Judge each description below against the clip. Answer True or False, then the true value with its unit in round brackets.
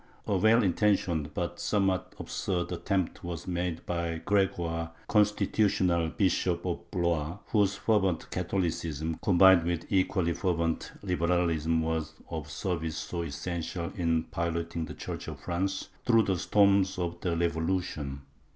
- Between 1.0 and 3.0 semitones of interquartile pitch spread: True (2.5 semitones)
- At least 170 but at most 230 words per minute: False (135 wpm)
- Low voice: True (85 Hz)